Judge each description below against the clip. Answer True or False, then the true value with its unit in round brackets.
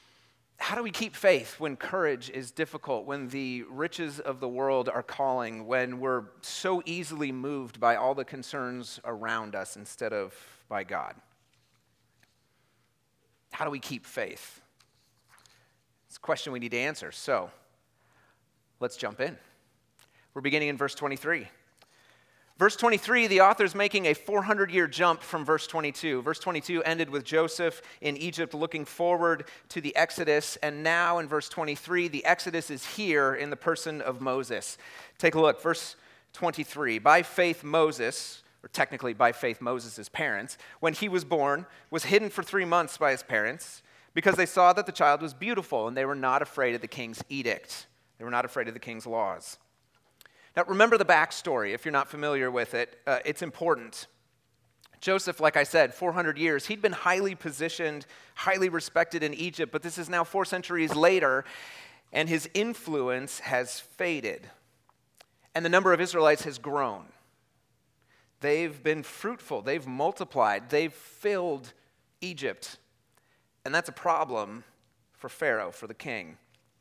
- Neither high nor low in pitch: True (155 Hz)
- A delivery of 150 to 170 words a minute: True (160 wpm)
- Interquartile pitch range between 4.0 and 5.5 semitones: True (4.5 semitones)